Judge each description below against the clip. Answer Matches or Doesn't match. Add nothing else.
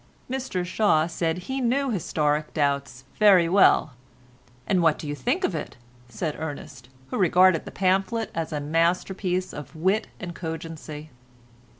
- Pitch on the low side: Doesn't match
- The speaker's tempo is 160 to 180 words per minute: Doesn't match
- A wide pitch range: Doesn't match